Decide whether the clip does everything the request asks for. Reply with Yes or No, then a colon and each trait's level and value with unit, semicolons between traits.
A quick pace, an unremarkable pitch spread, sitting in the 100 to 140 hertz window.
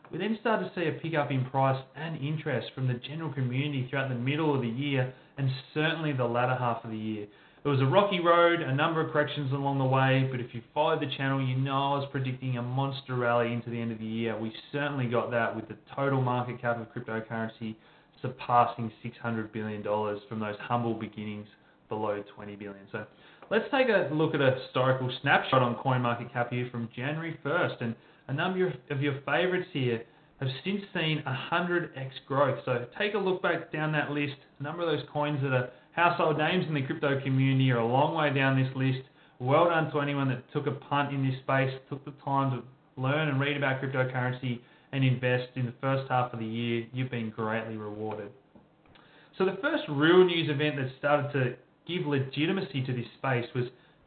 Yes: fast, 210 wpm; average, 3.6 semitones; low, 135 Hz